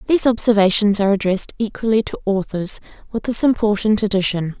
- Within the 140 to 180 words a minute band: Yes, average, 145 wpm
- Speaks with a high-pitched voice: Yes, high, 210 Hz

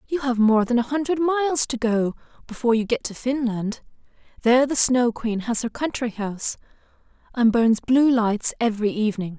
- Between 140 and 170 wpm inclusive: No, average, 180 wpm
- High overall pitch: Yes, high, 240 Hz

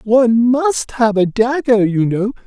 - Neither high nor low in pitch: No, high, 230 Hz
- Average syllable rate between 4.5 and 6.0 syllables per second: No, 4.0 syllables/s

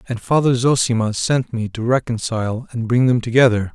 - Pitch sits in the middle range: No, low, 120 Hz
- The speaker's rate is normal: Yes, average, 175 wpm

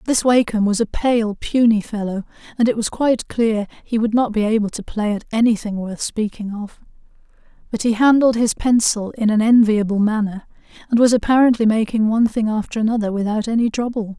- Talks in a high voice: Yes, high, 220 Hz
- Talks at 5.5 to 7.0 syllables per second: Yes, 5.6 syllables/s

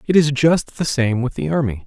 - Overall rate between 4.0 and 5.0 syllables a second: No, 5.3 syllables/s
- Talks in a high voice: No, low, 135 Hz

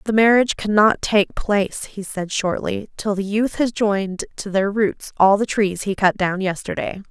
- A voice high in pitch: Yes, high, 200 Hz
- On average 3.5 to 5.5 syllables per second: Yes, 4.7 syllables/s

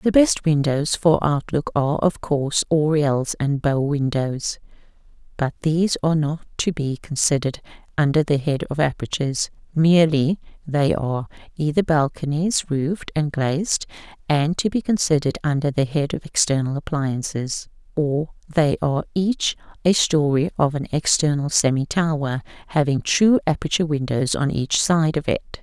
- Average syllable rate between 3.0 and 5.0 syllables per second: Yes, 4.8 syllables/s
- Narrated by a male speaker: No, female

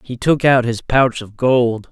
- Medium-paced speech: No, fast, 220 wpm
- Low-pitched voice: Yes, low, 120 Hz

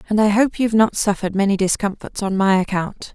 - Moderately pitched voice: No, high, 200 Hz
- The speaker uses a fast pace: Yes, fast, 210 wpm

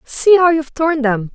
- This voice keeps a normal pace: No, fast, 225 wpm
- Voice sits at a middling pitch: No, very high, 290 Hz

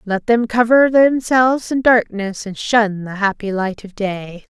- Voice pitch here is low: No, high, 220 Hz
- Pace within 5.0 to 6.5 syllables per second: No, 4.1 syllables/s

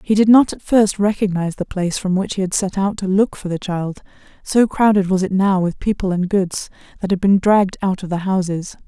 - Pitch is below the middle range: No, high, 190 Hz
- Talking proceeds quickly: Yes, fast, 245 wpm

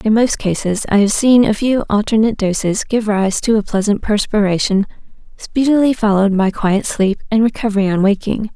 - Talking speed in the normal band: Yes, average, 175 wpm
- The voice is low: No, high, 210 Hz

